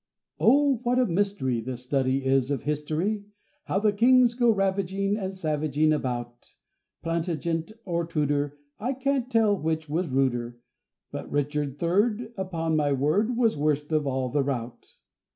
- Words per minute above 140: Yes, average, 150 wpm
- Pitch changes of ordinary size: No, wide, 6.4 semitones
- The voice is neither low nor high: Yes, medium, 160 Hz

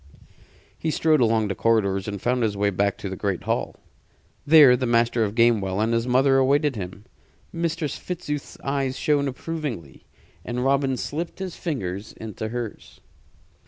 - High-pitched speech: No, low, 120 Hz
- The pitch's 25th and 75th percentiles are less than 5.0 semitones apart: No, wide, 5.5 semitones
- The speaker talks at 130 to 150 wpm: No, average, 160 wpm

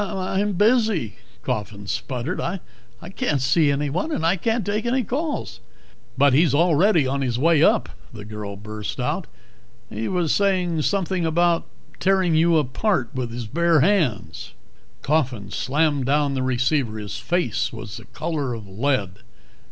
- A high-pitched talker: No, medium, 150 Hz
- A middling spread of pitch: No, wide, 6.8 semitones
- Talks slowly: No, average, 150 wpm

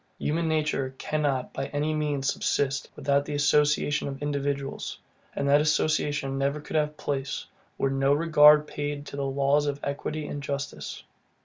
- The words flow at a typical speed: Yes, average, 155 wpm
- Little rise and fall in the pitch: Yes, narrow, 1.3 semitones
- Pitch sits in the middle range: Yes, medium, 145 Hz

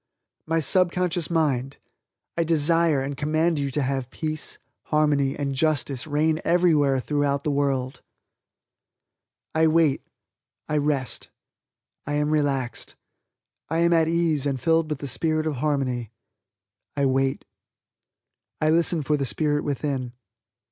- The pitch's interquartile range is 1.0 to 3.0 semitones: Yes, average, 2.7 semitones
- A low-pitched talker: No, medium, 150 Hz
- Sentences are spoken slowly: Yes, slow, 130 wpm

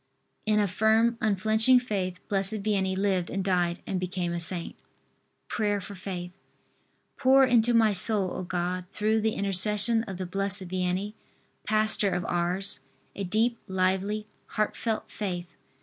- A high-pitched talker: Yes, high, 195 Hz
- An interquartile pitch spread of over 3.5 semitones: No, average, 2.9 semitones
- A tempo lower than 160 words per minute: Yes, average, 145 wpm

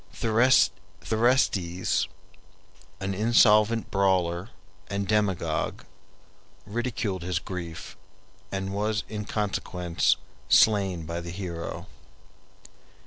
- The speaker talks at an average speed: No, slow, 80 wpm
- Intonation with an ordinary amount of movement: Yes, average, 3.3 semitones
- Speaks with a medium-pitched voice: No, low, 100 Hz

